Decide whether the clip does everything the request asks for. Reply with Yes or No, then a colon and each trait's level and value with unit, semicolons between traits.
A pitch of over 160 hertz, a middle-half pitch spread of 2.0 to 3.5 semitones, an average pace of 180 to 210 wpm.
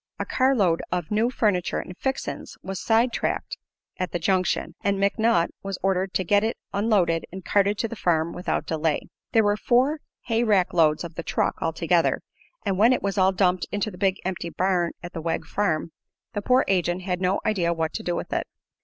Yes: high, 190 Hz; average, 3.2 semitones; average, 200 wpm